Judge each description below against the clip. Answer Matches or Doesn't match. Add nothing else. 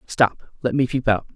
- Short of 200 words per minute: Doesn't match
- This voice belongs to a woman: Doesn't match